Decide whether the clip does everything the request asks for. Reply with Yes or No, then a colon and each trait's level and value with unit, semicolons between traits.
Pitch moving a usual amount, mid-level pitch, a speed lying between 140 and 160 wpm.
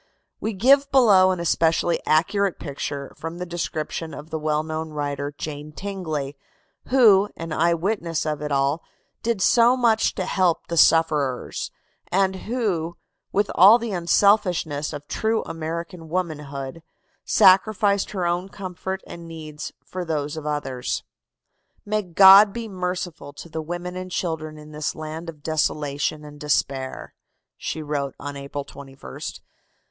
Yes: average, 4.1 semitones; medium, 165 Hz; average, 145 wpm